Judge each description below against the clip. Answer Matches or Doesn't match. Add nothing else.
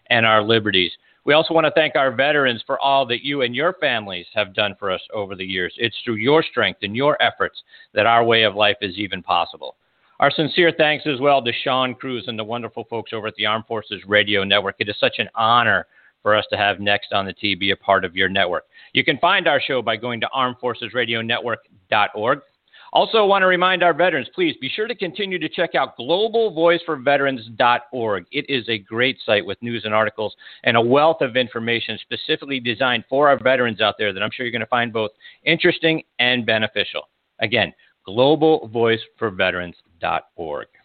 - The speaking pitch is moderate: Doesn't match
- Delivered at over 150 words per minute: Matches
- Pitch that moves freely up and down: Matches